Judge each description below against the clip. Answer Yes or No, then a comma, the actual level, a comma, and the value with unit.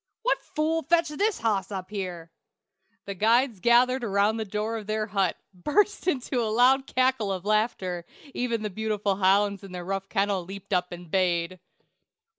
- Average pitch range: Yes, average, 4.2 semitones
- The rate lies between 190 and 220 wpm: No, average, 170 wpm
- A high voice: Yes, high, 210 Hz